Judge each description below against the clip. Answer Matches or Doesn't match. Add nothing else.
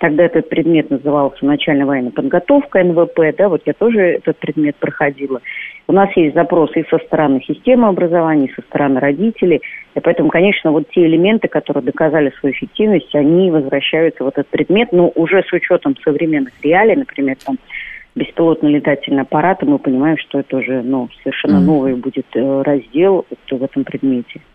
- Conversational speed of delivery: Doesn't match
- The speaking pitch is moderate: Matches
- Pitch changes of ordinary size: Matches